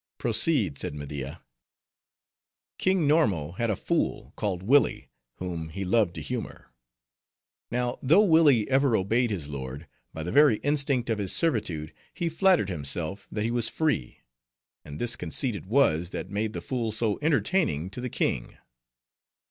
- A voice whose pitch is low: Yes, low, 110 Hz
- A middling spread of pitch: No, wide, 8.1 semitones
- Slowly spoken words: No, average, 155 wpm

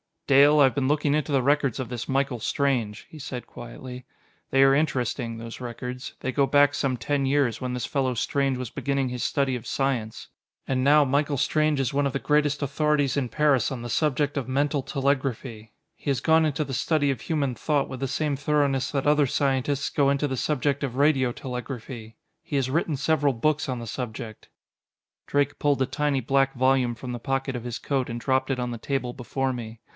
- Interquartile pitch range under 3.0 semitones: Yes, narrow, 2.4 semitones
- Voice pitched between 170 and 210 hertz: No, low, 135 Hz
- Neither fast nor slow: No, fast, 210 wpm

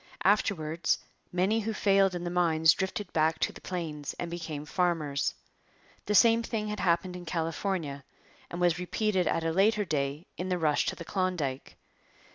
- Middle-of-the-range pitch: Yes, medium, 175 Hz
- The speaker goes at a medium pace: Yes, average, 170 wpm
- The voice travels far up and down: No, average, 3.3 semitones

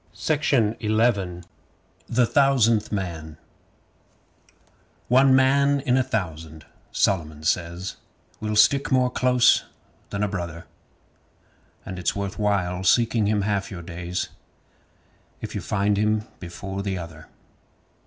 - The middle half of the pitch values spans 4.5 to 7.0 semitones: Yes, average, 4.9 semitones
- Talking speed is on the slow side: Yes, slow, 115 wpm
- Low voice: Yes, low, 100 Hz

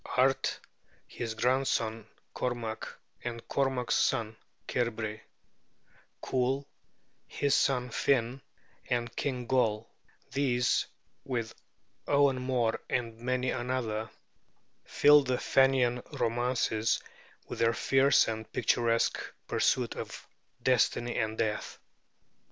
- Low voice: Yes, low, 125 Hz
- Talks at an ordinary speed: No, slow, 95 wpm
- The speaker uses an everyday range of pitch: No, narrow, 2.3 semitones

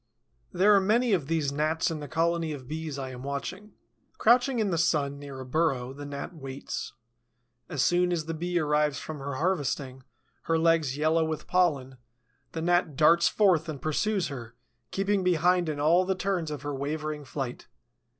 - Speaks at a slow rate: No, average, 180 wpm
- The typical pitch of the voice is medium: Yes, medium, 155 Hz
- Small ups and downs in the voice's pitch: No, average, 3.9 semitones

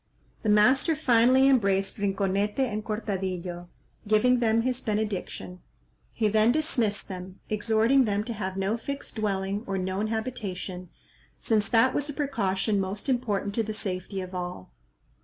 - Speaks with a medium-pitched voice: No, high, 210 Hz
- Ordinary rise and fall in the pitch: Yes, average, 3.4 semitones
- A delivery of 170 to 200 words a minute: No, average, 145 wpm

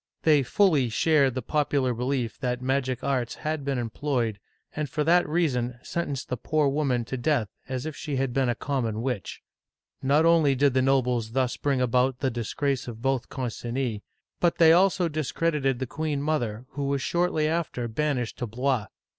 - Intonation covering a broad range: No, average, 3.5 semitones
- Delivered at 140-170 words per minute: No, average, 180 wpm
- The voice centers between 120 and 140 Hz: Yes, low, 135 Hz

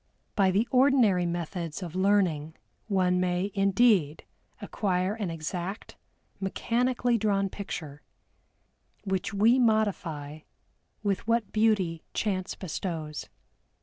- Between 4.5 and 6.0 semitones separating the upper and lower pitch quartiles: No, average, 3.7 semitones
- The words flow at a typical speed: No, slow, 100 wpm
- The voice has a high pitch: Yes, high, 195 Hz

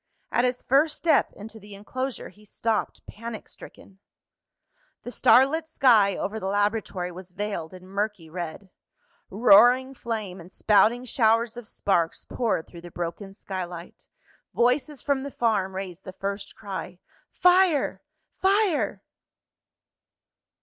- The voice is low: No, high, 210 Hz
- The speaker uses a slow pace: Yes, slow, 130 wpm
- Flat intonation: No, average, 4.7 semitones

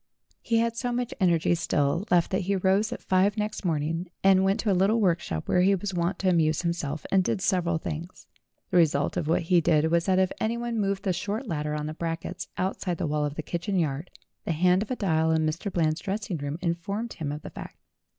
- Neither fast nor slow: No, fast, 230 wpm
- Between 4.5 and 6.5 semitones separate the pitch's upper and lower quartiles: No, average, 3.5 semitones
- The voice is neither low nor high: Yes, medium, 180 Hz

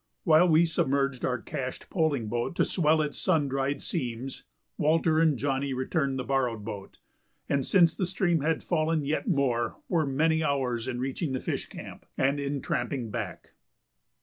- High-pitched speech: No, medium, 140 Hz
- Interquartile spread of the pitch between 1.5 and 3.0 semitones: No, average, 3.5 semitones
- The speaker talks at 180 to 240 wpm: No, average, 170 wpm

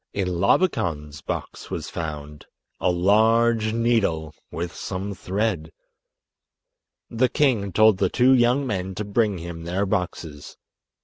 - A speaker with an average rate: No, slow, 120 wpm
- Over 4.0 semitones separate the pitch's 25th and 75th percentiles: Yes, average, 4.8 semitones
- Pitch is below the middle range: Yes, very low, 95 Hz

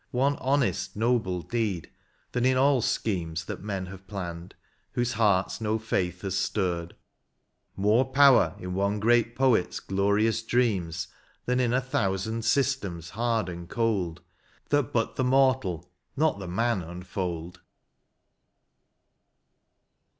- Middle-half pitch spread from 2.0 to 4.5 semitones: No, average, 5.0 semitones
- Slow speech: Yes, slow, 130 wpm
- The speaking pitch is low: Yes, low, 105 Hz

